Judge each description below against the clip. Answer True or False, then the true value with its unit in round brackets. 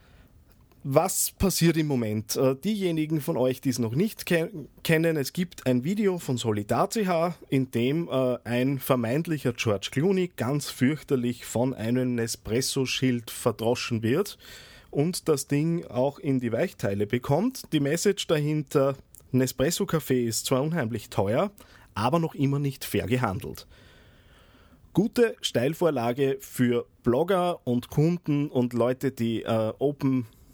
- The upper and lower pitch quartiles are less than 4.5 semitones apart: False (5.2 semitones)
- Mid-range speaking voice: False (130 Hz)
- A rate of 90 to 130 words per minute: True (125 wpm)